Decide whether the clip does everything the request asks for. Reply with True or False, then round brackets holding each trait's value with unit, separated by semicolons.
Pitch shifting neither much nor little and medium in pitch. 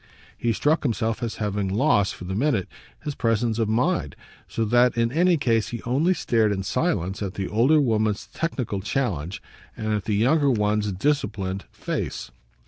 False (4.5 semitones; 115 Hz)